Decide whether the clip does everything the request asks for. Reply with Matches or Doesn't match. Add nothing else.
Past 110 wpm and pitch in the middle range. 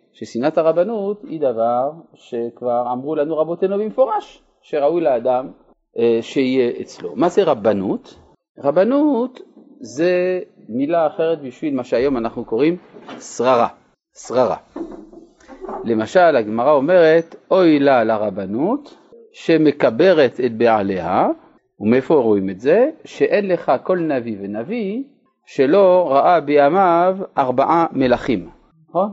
Doesn't match